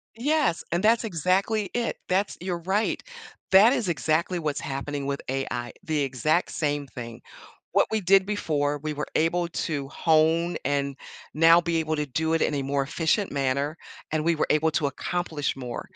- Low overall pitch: No, medium, 160 Hz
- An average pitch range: Yes, average, 3.9 semitones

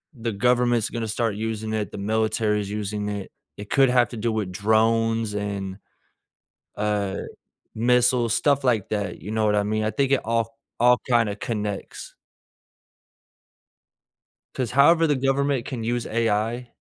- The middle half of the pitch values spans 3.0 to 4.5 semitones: No, narrow, 2.6 semitones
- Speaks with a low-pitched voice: Yes, low, 110 Hz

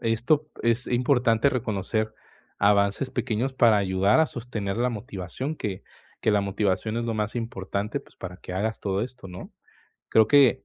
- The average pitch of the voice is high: No, low, 110 Hz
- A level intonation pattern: No, average, 3.7 semitones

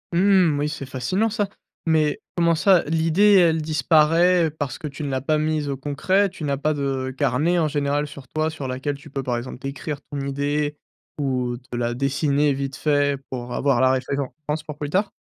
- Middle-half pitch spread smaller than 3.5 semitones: Yes, narrow, 2.6 semitones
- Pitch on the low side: No, medium, 145 Hz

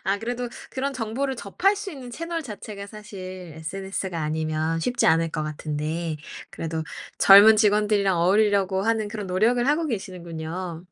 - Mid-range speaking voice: No, high, 200 Hz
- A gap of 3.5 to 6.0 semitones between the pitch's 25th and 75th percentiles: Yes, average, 5.3 semitones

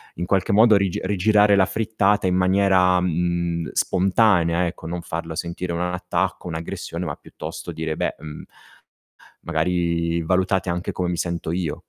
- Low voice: Yes, very low, 90 Hz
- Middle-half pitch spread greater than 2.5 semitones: No, narrow, 2.0 semitones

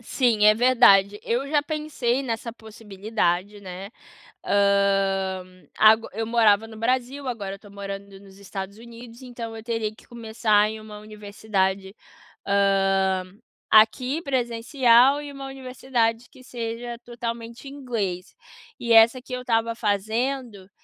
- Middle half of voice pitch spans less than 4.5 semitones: Yes, average, 3.3 semitones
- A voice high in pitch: Yes, high, 225 Hz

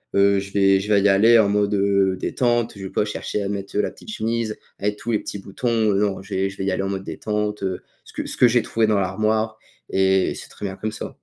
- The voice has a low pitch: Yes, low, 100 Hz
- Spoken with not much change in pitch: Yes, narrow, 1.9 semitones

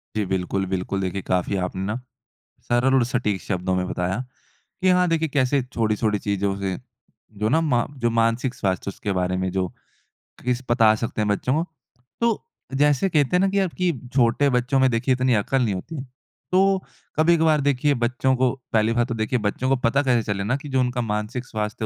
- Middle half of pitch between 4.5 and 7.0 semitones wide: Yes, average, 5.0 semitones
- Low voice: Yes, low, 120 Hz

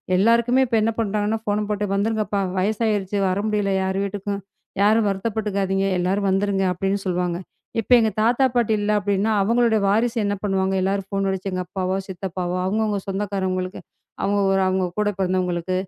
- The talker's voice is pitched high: Yes, high, 200 Hz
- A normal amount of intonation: No, narrow, 2.0 semitones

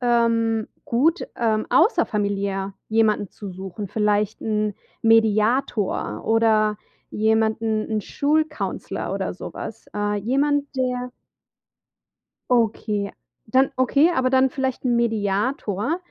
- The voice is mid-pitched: No, high, 225 Hz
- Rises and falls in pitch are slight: No, average, 3.4 semitones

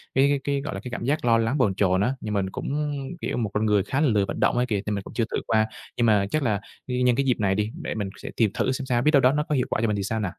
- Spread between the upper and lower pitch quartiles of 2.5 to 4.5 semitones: Yes, average, 4.2 semitones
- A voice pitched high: No, low, 115 Hz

